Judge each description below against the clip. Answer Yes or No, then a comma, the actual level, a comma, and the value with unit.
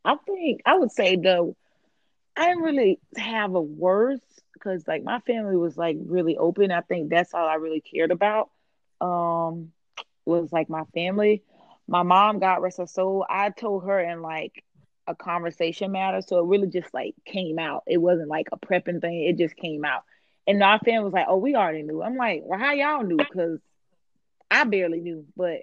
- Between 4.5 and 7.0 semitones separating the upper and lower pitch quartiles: No, average, 3.3 semitones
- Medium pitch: Yes, medium, 180 Hz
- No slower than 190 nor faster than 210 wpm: Yes, average, 195 wpm